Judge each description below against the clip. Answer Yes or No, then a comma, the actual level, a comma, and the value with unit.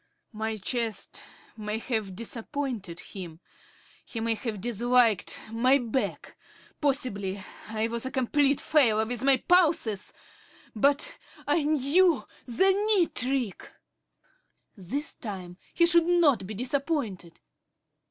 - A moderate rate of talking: No, slow, 115 wpm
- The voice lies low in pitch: No, high, 240 Hz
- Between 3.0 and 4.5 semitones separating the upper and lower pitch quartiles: No, average, 5.0 semitones